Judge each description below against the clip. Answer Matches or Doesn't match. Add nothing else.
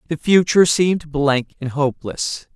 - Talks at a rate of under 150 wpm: Matches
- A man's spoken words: Matches